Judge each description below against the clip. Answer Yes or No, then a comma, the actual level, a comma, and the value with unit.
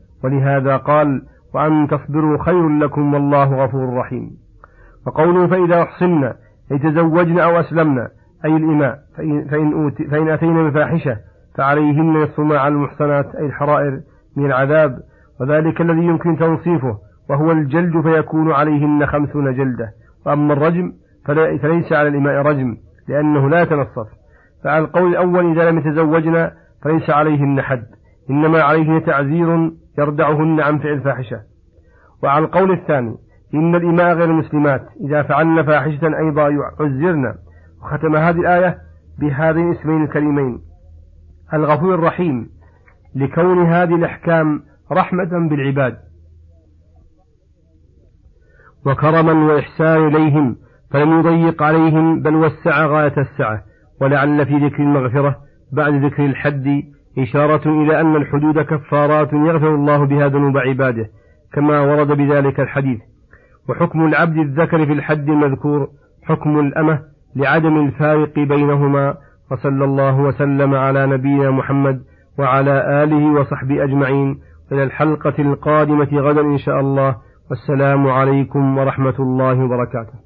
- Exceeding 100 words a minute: Yes, average, 115 wpm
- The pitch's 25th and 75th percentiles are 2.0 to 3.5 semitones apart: Yes, narrow, 2.6 semitones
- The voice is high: No, medium, 145 Hz